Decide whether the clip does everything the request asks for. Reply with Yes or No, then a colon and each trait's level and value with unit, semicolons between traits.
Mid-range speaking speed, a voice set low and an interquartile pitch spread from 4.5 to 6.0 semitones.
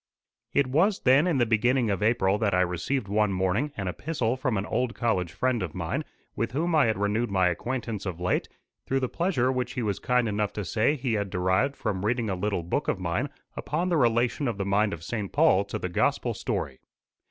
No: fast, 220 wpm; low, 110 Hz; average, 4.8 semitones